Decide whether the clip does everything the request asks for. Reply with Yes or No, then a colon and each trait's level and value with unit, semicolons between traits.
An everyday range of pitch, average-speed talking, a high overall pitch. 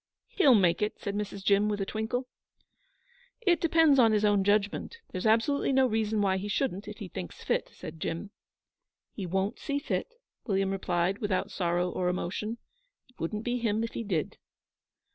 Yes: average, 3.5 semitones; average, 180 wpm; high, 210 Hz